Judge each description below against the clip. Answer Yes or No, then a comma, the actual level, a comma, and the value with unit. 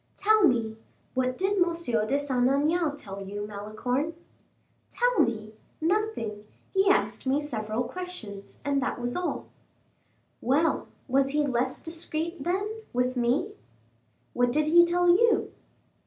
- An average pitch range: No, wide, 6.2 semitones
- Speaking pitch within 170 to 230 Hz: No, very high, 280 Hz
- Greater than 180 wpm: No, slow, 135 wpm